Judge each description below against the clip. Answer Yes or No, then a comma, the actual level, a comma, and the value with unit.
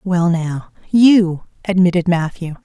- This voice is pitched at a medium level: Yes, medium, 180 Hz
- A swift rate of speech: No, slow, 115 wpm